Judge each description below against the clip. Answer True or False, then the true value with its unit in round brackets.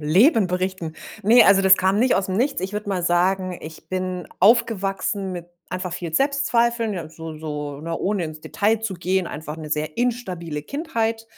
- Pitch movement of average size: True (5.0 semitones)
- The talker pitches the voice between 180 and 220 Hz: True (185 Hz)